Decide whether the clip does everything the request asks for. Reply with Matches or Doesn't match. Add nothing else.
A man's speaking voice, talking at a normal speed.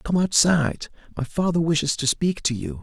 Matches